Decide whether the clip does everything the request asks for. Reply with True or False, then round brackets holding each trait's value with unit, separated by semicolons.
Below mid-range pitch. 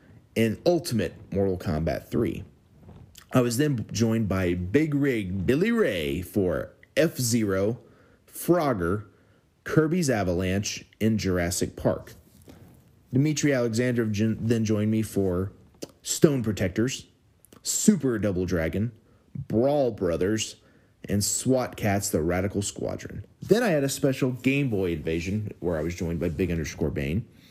True (110 Hz)